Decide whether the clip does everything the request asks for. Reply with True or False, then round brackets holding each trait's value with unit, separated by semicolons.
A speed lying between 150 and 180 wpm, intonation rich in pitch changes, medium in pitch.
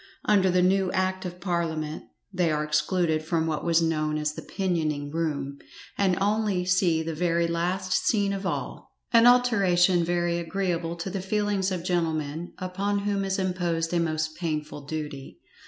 False (165 wpm; 3.0 semitones; 175 Hz)